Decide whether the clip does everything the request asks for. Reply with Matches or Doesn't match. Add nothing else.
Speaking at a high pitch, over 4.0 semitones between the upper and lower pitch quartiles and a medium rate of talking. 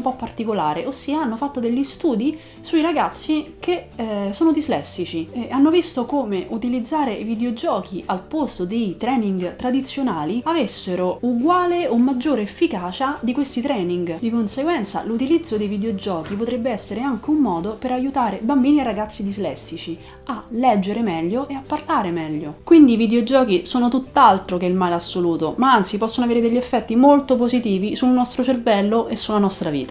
Matches